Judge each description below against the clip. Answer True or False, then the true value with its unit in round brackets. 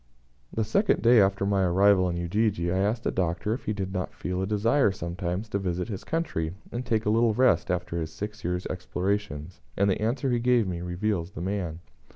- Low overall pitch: True (95 Hz)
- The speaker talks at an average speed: False (215 wpm)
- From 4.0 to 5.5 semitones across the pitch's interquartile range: False (3.5 semitones)